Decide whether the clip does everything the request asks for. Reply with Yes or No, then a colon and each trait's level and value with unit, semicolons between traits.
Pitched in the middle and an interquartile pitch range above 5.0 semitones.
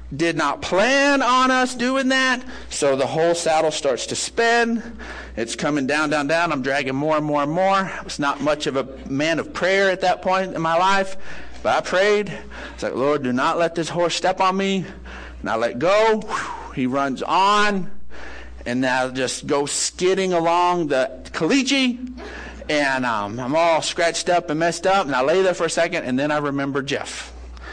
Yes: medium, 170 Hz; wide, 5.4 semitones